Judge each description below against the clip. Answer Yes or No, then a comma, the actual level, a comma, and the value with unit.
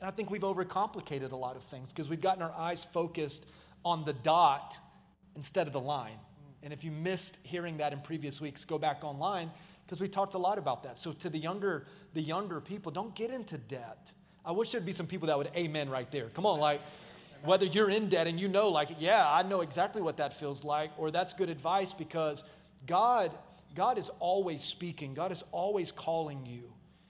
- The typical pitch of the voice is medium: Yes, medium, 165 Hz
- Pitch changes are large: No, average, 4.0 semitones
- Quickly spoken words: Yes, fast, 215 wpm